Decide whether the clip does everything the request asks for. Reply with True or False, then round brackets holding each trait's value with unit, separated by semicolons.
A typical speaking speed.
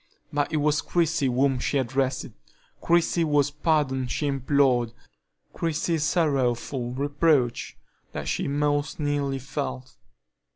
False (115 wpm)